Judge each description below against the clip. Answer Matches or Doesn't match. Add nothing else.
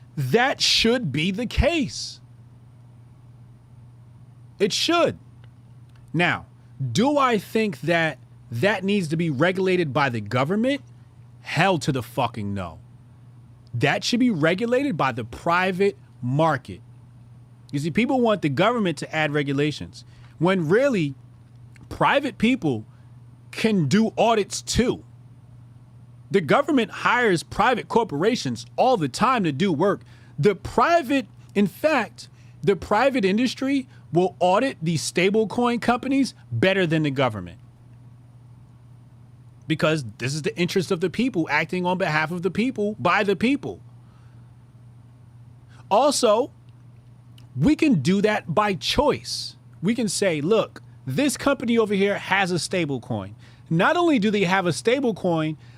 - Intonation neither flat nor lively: Doesn't match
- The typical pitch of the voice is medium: Matches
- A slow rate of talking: Matches